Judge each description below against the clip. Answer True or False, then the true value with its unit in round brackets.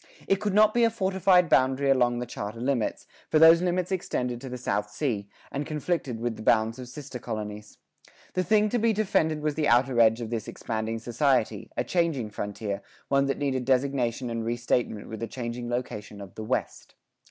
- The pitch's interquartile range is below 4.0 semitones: False (5.5 semitones)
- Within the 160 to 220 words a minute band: True (200 wpm)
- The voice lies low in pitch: True (125 Hz)